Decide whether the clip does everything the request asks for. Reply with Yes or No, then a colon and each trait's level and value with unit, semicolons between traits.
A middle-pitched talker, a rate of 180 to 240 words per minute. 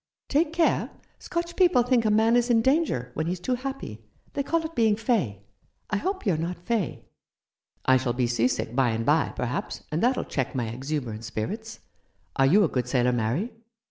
Yes: medium, 180 Hz; average, 195 wpm